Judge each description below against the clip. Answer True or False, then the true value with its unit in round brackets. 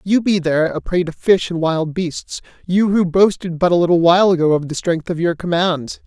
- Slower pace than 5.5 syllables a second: True (5.3 syllables/s)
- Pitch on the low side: False (175 Hz)